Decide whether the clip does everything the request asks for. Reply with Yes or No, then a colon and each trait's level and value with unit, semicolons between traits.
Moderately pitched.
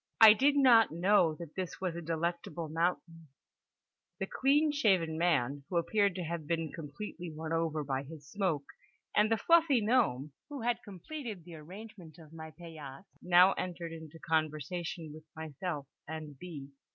Yes: medium, 170 Hz